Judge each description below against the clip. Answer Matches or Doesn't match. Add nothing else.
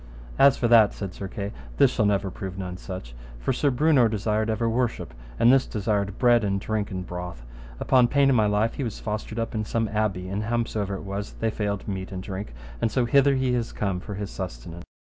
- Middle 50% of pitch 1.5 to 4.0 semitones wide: Matches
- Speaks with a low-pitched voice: Matches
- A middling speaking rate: Doesn't match